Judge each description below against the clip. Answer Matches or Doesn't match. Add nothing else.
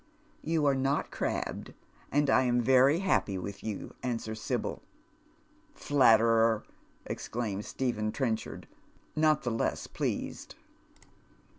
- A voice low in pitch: Matches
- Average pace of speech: Doesn't match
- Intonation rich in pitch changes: Doesn't match